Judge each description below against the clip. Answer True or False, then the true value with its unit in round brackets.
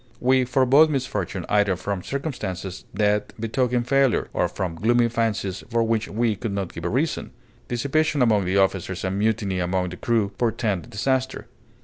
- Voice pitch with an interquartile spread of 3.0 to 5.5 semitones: True (4.5 semitones)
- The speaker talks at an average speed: True (160 wpm)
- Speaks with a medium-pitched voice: False (110 Hz)